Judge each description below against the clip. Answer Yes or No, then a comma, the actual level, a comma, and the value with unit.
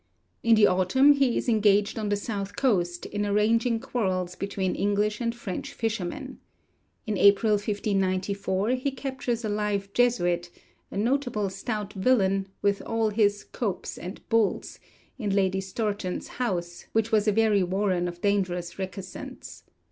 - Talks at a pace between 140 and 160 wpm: Yes, average, 145 wpm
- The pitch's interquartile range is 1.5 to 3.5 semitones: Yes, average, 2.9 semitones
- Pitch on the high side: Yes, high, 205 Hz